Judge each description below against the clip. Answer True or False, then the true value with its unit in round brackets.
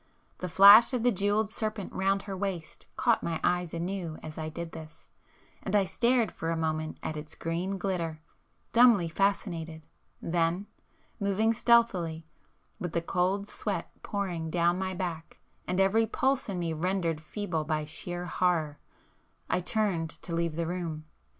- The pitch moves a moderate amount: True (3.4 semitones)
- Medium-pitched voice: True (180 Hz)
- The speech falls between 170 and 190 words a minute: False (155 wpm)